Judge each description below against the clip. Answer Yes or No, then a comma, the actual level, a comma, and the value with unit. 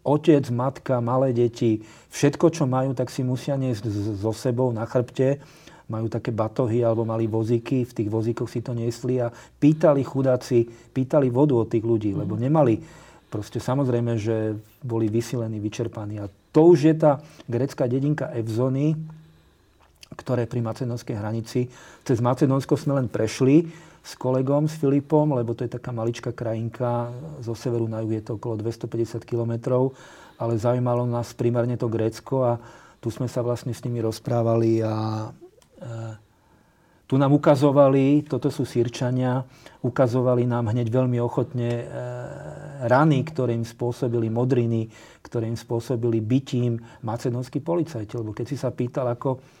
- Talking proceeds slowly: No, average, 150 wpm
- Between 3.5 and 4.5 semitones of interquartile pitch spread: No, narrow, 2.5 semitones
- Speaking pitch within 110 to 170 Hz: Yes, low, 120 Hz